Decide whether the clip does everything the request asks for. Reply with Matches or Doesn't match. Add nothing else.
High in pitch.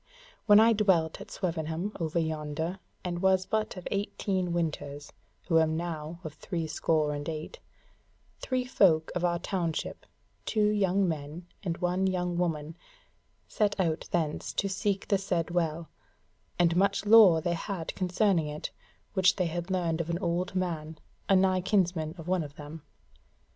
Doesn't match